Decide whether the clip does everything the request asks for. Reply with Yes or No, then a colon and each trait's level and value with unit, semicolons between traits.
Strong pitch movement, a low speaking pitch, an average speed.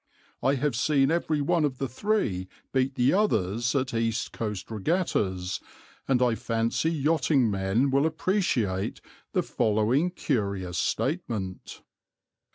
No: wide, 5.9 semitones; low, 125 Hz; slow, 125 wpm